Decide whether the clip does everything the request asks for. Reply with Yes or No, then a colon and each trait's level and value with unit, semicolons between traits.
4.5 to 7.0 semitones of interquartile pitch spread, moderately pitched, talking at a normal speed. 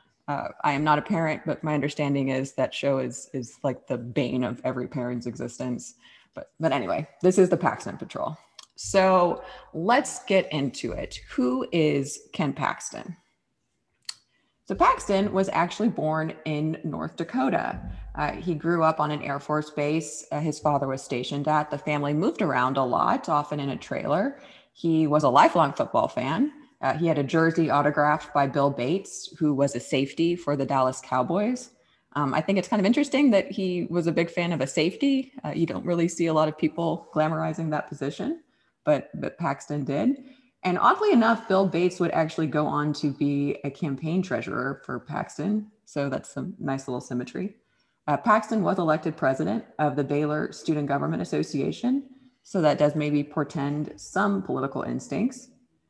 Yes: average, 4.8 semitones; medium, 155 Hz; average, 180 wpm